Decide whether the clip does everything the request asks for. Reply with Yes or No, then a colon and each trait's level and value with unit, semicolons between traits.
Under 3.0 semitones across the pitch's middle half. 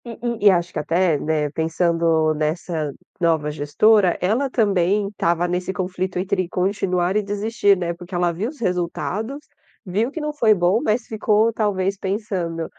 No: average, 3.7 semitones